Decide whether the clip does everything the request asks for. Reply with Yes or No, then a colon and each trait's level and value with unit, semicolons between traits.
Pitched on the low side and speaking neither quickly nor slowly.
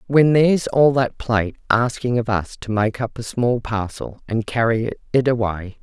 Yes: low, 115 Hz; average, 185 wpm